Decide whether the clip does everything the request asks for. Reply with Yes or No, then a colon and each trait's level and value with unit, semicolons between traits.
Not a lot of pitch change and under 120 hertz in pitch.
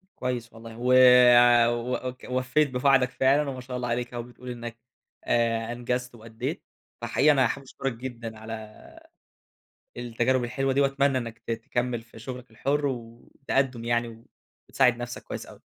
No: narrow, 1.9 semitones; low, 125 Hz